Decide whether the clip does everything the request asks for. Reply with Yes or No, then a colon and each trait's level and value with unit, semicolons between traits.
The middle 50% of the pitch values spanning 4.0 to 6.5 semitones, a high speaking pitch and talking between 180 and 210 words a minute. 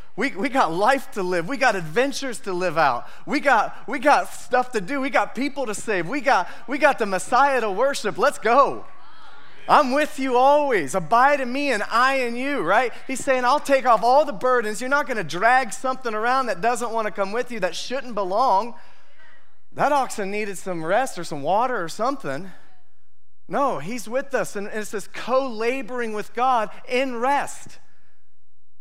Yes: average, 4.3 semitones; high, 245 Hz; average, 195 wpm